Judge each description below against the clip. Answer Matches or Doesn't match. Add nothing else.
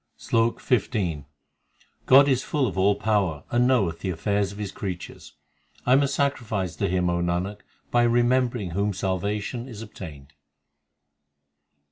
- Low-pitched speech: Matches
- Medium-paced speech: Matches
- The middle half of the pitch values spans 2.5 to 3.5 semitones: Doesn't match